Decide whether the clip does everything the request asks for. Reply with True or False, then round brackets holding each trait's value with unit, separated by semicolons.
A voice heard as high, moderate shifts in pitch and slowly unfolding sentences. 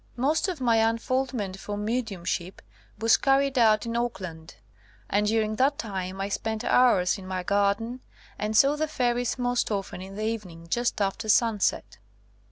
False (220 Hz; 3.9 semitones; 170 wpm)